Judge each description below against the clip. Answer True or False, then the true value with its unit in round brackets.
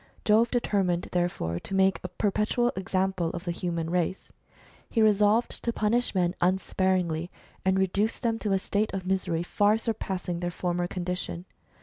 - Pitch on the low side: False (190 Hz)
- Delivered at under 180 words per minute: True (155 wpm)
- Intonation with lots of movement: False (3.1 semitones)